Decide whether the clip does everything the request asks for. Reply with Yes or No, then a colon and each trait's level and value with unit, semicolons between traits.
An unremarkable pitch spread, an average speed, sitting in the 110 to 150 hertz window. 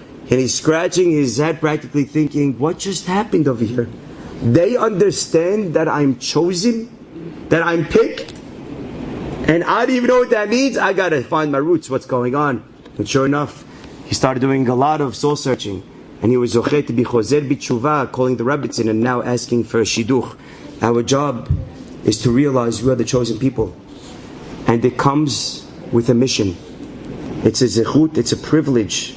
Yes: average, 4.2 semitones; average, 170 wpm; low, 135 Hz